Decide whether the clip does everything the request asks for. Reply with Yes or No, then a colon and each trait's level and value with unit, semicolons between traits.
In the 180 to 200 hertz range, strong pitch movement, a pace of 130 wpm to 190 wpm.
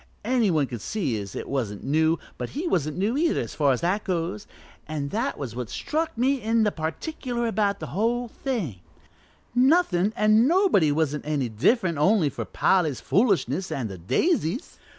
Yes: medium, 185 Hz; wide, 8.6 semitones; average, 170 wpm